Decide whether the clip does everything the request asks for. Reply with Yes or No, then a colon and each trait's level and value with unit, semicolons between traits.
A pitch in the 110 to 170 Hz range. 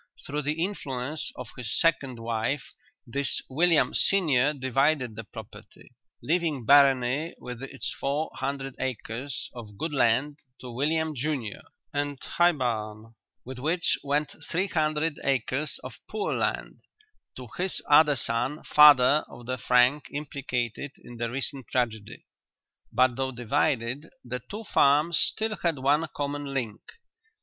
Yes: low, 135 Hz